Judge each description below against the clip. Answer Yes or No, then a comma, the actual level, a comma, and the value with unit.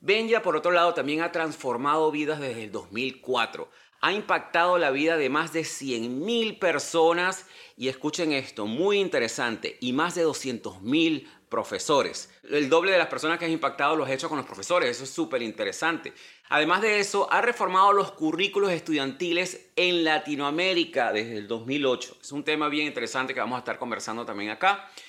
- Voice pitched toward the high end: No, medium, 165 Hz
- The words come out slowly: No, average, 175 wpm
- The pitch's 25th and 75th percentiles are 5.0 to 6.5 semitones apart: Yes, wide, 5.4 semitones